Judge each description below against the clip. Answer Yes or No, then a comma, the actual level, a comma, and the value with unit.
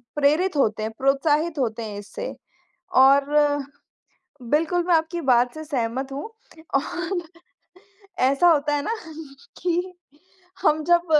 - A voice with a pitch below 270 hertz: No, very high, 295 Hz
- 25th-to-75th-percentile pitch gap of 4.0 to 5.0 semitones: Yes, average, 4.3 semitones